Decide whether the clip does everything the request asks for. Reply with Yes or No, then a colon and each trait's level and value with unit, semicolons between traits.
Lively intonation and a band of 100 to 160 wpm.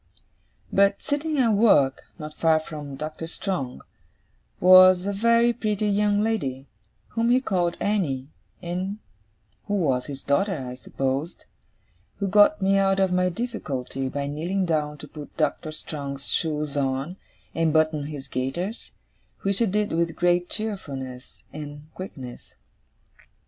Yes: wide, 5.8 semitones; average, 140 wpm